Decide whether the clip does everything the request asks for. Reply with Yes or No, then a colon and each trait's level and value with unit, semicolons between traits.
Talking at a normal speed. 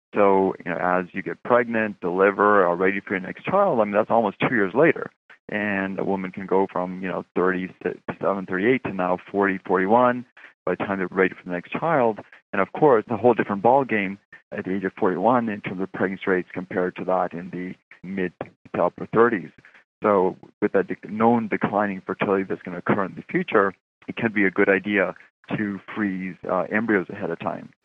No: fast, 210 wpm